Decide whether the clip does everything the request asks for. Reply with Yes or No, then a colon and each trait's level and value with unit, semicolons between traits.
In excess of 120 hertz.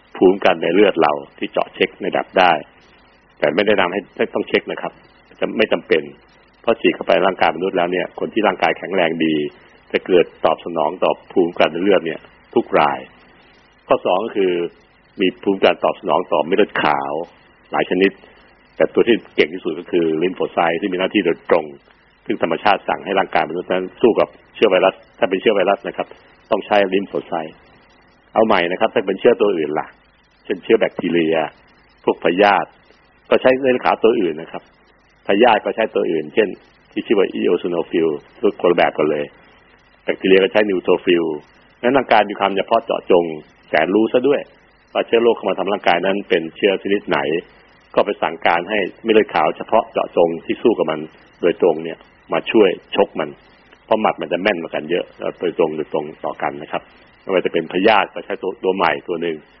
No: very low, 95 Hz